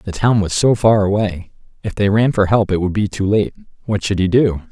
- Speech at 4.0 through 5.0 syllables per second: No, 5.3 syllables/s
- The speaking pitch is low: Yes, low, 100 Hz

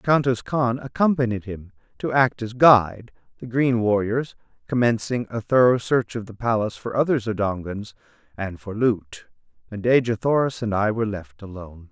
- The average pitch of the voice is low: Yes, low, 115 Hz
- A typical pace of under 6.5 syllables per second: Yes, 5.0 syllables/s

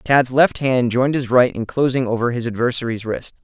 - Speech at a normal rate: No, fast, 210 wpm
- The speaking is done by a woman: No, male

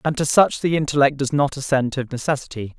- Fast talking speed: Yes, fast, 215 wpm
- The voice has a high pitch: No, medium, 140 Hz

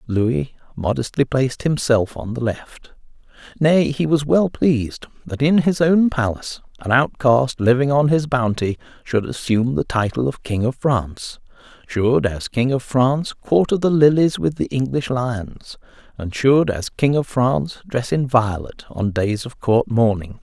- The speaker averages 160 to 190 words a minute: Yes, average, 165 wpm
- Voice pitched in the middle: No, low, 125 Hz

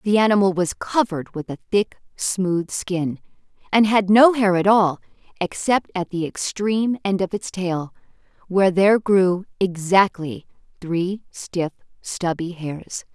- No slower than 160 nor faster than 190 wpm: No, average, 140 wpm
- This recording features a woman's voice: Yes, female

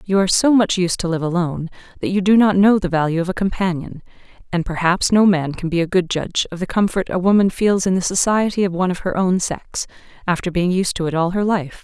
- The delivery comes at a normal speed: No, fast, 255 wpm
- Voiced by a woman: Yes, female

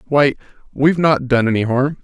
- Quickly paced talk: No, average, 175 wpm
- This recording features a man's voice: Yes, male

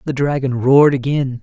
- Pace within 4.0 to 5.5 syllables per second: Yes, 5.4 syllables/s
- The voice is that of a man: Yes, male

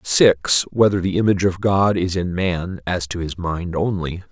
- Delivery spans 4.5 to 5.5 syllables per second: Yes, 4.9 syllables/s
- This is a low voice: Yes, very low, 90 Hz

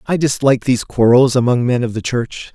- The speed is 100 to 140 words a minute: No, fast, 210 wpm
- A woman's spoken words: No, male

